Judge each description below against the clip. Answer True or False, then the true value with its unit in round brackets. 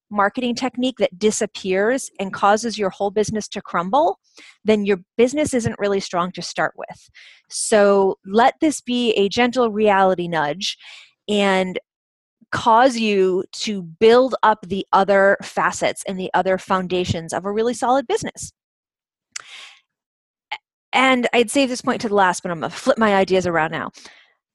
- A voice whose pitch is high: True (205 Hz)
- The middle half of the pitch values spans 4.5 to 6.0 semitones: False (4.0 semitones)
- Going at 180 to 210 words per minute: False (155 wpm)